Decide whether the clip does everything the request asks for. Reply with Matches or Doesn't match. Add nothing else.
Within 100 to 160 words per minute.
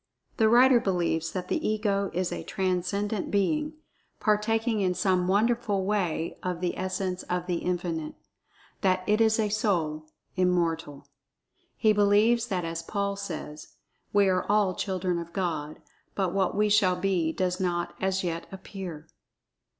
Matches